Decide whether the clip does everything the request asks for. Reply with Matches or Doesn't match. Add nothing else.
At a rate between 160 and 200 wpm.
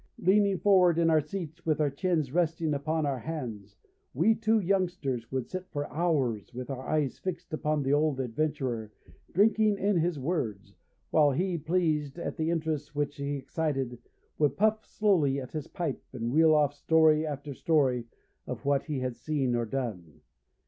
Matches